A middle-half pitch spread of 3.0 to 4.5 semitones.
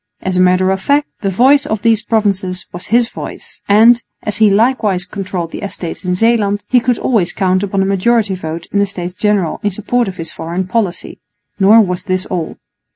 Yes: average, 3.4 semitones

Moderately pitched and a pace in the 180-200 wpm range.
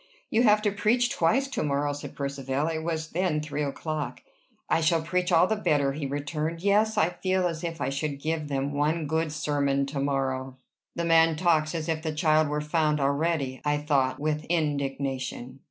Yes: medium, 155 Hz; average, 190 wpm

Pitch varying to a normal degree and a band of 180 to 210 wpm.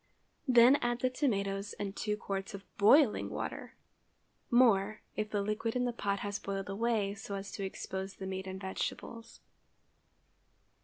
No: average, 3.0 semitones; average, 150 wpm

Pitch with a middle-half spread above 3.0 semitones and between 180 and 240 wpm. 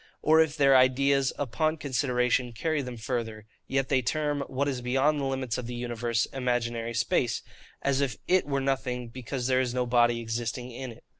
No: narrow, 2.4 semitones; average, 190 wpm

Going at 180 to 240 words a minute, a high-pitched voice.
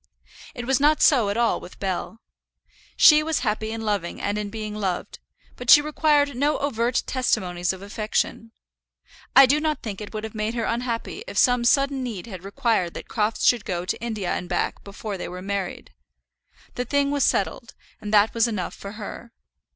Yes: average, 190 wpm; high, 225 Hz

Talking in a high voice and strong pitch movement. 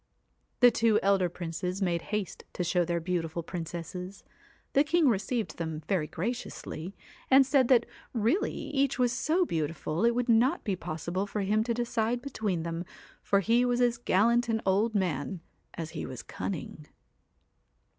Yes: high, 200 Hz; wide, 5.7 semitones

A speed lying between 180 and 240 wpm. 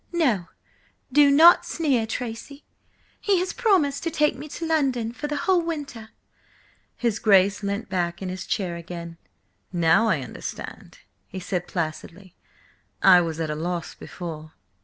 No: average, 150 wpm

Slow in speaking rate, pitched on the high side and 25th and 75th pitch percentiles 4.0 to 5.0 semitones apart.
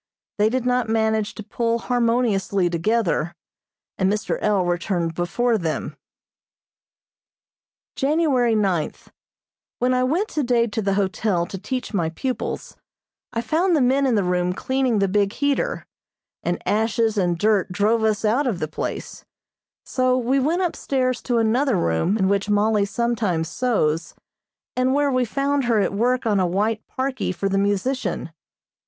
No: average, 155 wpm; high, 220 Hz; average, 4.5 semitones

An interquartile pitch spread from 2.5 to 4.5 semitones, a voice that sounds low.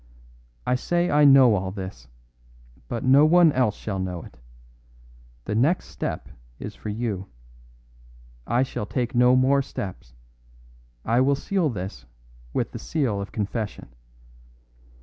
No: wide, 5.6 semitones; low, 120 Hz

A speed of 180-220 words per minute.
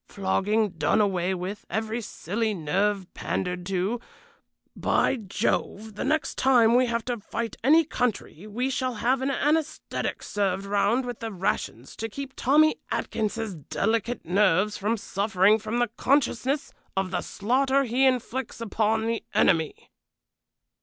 No: average, 140 wpm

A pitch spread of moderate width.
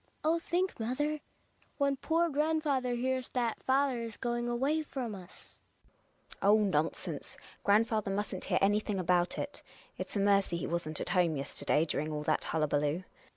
No: wide, 7.0 semitones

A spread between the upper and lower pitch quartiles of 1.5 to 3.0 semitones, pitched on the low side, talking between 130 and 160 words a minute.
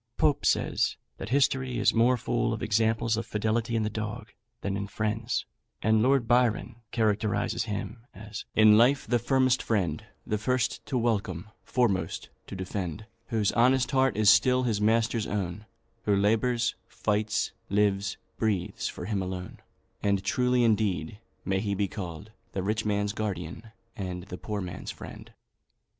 Yes: average, 2.7 semitones; low, 110 Hz; average, 155 wpm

